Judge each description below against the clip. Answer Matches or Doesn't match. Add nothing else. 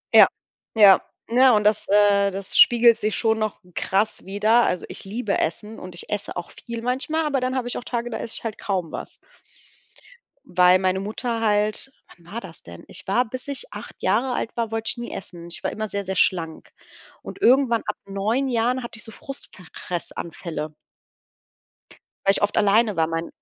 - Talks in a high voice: Matches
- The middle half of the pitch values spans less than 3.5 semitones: Doesn't match